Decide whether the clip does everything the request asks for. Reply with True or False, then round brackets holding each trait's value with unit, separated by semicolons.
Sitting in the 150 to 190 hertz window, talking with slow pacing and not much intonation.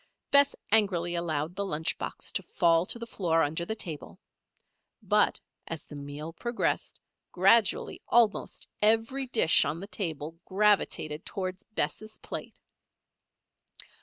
False (185 Hz; 130 wpm; 5.0 semitones)